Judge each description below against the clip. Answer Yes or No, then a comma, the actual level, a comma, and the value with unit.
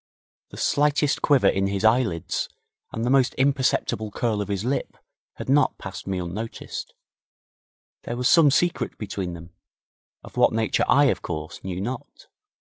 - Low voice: Yes, low, 110 Hz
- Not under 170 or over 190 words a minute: No, average, 155 wpm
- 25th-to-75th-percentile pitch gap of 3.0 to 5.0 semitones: No, wide, 5.6 semitones